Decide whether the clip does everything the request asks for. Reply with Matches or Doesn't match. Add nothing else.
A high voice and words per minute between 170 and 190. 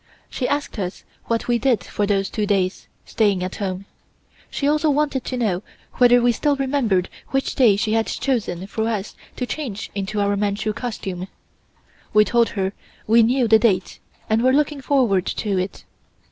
Matches